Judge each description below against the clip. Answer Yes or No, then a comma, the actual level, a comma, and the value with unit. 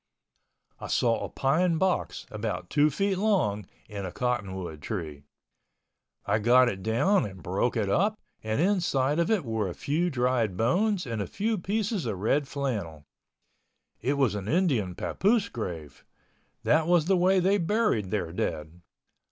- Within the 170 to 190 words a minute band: No, average, 155 wpm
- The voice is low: Yes, low, 125 Hz